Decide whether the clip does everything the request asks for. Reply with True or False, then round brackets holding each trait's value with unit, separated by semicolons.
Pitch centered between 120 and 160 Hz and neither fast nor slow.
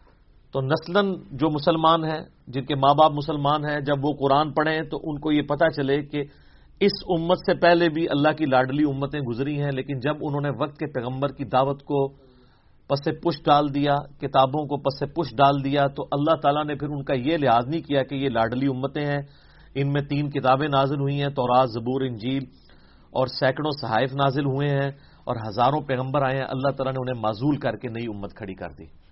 False (140 Hz; 215 wpm)